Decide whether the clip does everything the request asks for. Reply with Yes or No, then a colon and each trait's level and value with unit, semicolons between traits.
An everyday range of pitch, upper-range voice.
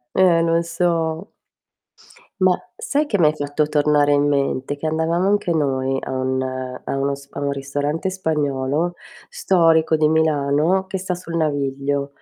No: average, 3.3 semitones; medium, 155 Hz